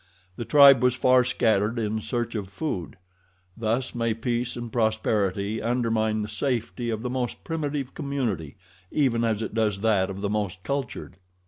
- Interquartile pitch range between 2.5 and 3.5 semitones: Yes, average, 2.9 semitones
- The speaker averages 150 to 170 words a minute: Yes, average, 160 wpm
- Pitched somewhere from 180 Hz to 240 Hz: No, low, 115 Hz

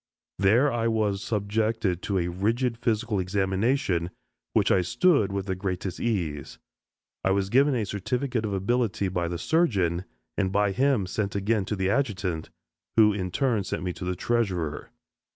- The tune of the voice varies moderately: Yes, average, 3.7 semitones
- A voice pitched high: No, low, 100 Hz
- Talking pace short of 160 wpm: No, average, 165 wpm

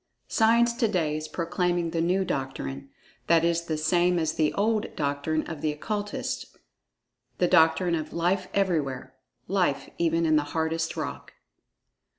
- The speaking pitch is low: No, medium, 165 Hz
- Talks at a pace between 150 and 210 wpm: No, slow, 135 wpm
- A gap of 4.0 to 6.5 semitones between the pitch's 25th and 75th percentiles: No, average, 2.9 semitones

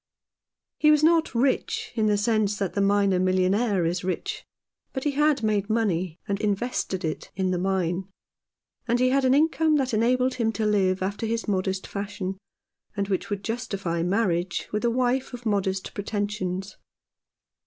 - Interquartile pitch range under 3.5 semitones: No, average, 4.4 semitones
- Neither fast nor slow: Yes, average, 165 wpm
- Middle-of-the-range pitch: No, high, 205 Hz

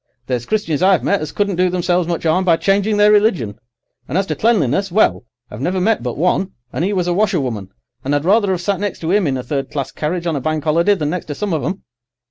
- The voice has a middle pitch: Yes, medium, 175 Hz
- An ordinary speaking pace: No, fast, 255 wpm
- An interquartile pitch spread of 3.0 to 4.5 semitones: No, average, 4.9 semitones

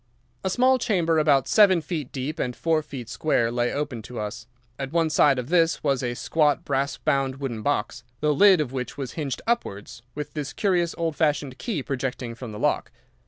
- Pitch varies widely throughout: No, average, 4.4 semitones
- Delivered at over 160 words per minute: Yes, average, 200 wpm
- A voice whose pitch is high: No, medium, 145 Hz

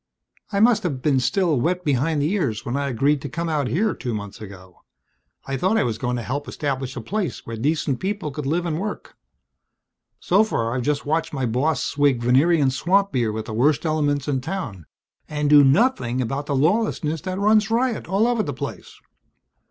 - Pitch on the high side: No, medium, 145 Hz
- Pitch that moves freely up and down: Yes, wide, 5.9 semitones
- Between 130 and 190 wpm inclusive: No, average, 200 wpm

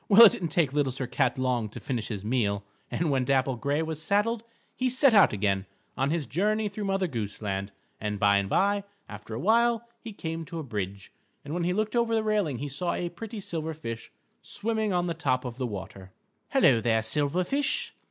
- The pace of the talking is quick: Yes, fast, 215 wpm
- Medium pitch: Yes, medium, 150 Hz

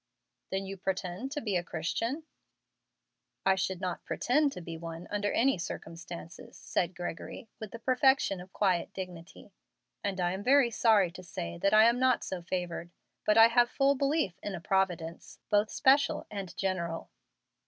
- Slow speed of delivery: No, average, 170 wpm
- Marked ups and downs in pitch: No, average, 4.8 semitones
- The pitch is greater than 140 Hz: Yes, high, 190 Hz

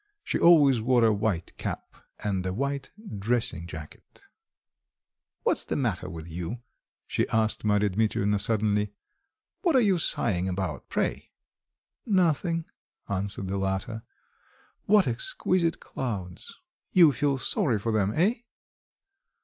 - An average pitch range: No, wide, 6.5 semitones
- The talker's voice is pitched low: Yes, low, 110 Hz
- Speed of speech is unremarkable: No, slow, 125 wpm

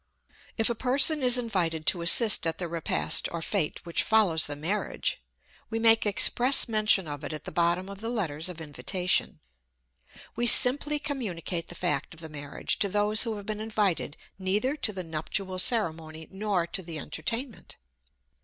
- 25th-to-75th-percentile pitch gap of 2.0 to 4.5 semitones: No, average, 5.3 semitones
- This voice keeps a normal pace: Yes, average, 175 wpm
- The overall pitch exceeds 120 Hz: Yes, high, 190 Hz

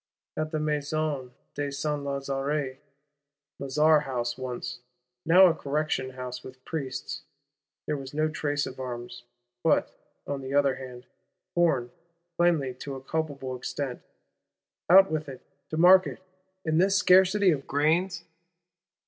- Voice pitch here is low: No, medium, 145 Hz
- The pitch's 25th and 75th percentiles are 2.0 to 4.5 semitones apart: Yes, average, 3.2 semitones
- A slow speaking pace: Yes, slow, 130 wpm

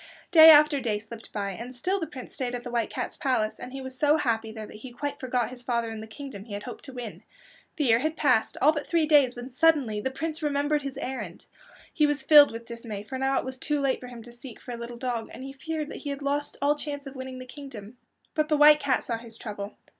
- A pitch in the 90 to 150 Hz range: No, very high, 260 Hz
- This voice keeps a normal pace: No, fast, 265 wpm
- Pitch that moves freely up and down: No, average, 3.8 semitones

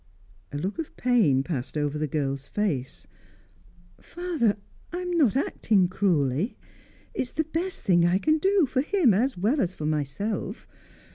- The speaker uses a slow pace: No, average, 160 wpm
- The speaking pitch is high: Yes, high, 205 Hz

